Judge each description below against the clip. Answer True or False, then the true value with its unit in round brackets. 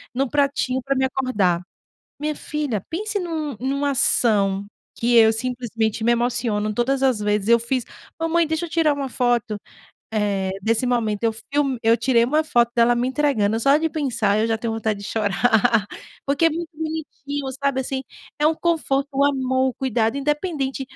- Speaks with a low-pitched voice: False (255 Hz)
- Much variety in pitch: False (4.2 semitones)